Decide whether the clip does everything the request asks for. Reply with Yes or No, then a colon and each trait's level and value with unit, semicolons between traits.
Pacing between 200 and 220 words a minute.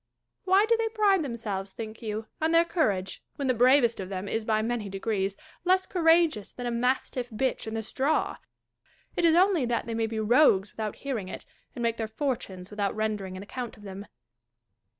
Yes: fast, 205 wpm